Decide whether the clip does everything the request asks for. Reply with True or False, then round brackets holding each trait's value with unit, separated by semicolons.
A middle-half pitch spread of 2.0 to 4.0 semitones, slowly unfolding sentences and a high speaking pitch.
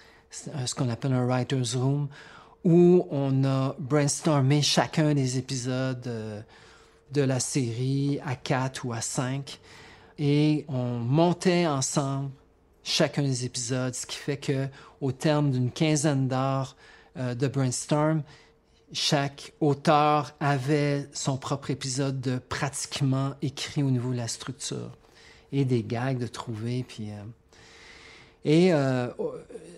False (2.7 semitones; 125 wpm; 135 Hz)